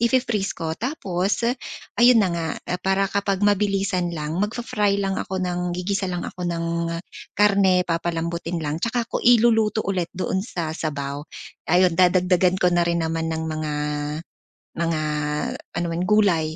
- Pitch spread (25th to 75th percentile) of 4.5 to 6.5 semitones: No, average, 3.2 semitones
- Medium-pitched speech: Yes, medium, 180 Hz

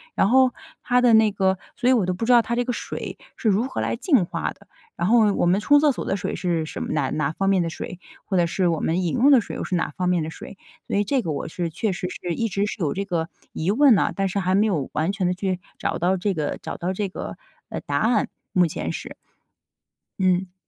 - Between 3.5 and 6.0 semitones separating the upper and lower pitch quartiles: Yes, average, 4.1 semitones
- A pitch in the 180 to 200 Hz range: Yes, high, 190 Hz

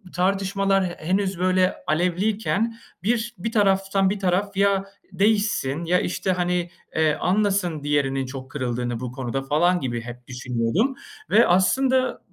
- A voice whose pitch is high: No, medium, 180 Hz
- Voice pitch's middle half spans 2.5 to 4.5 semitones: No, wide, 5.6 semitones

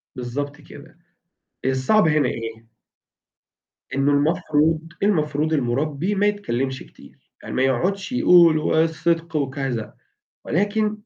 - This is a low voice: No, medium, 155 Hz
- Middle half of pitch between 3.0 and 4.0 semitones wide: No, average, 4.4 semitones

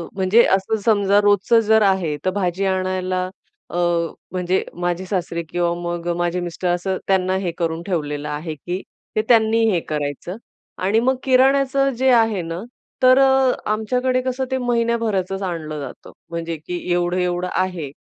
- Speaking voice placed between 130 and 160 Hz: No, medium, 185 Hz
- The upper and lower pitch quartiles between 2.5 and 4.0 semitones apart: No, average, 4.4 semitones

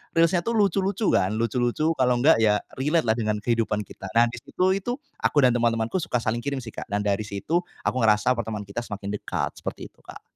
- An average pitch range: No, wide, 7.0 semitones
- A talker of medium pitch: No, low, 120 Hz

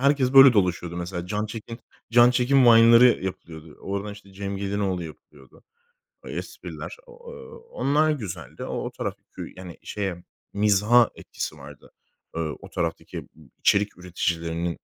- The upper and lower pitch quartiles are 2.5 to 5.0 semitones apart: No, wide, 5.4 semitones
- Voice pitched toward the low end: Yes, low, 100 Hz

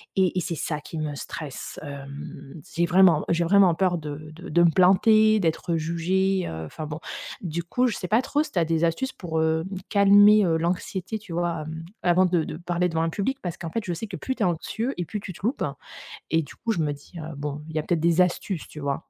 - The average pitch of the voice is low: No, medium, 170 Hz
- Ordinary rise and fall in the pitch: Yes, average, 3.1 semitones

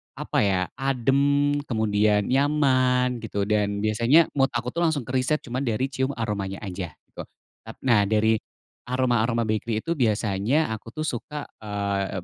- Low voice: Yes, low, 120 Hz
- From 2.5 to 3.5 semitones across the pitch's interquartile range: No, average, 4.3 semitones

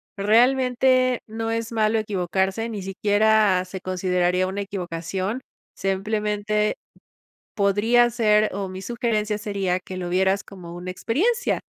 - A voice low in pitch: No, high, 205 Hz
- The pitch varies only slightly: No, average, 3.1 semitones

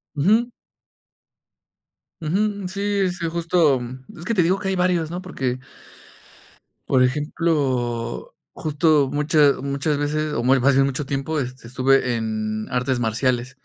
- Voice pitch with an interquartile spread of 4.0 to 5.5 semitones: Yes, average, 4.9 semitones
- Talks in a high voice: No, medium, 145 Hz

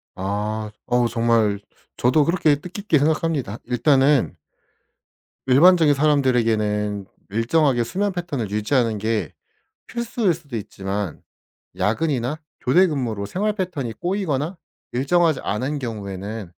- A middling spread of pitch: No, wide, 6.7 semitones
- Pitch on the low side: Yes, low, 130 Hz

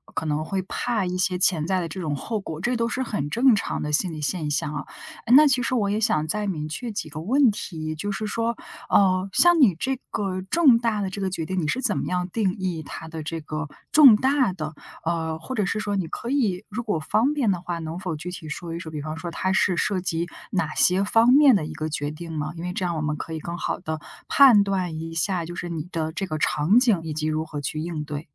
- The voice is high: No, medium, 180 Hz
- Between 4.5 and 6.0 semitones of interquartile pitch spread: Yes, average, 5.1 semitones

